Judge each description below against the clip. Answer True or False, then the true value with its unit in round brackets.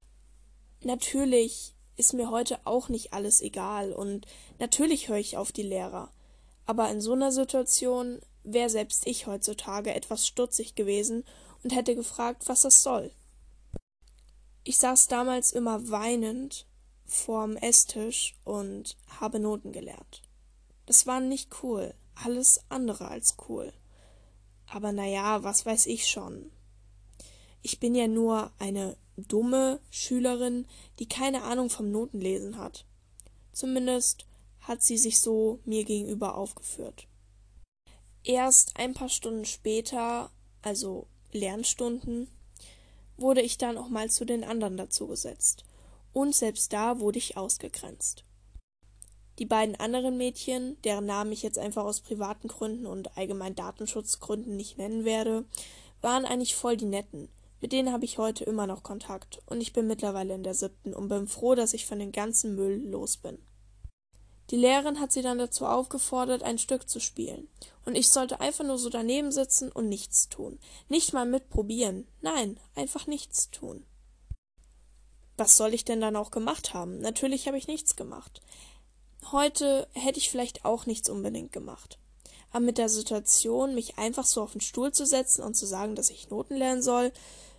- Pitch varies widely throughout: False (4.0 semitones)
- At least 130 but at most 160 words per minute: True (150 wpm)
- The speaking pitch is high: True (220 Hz)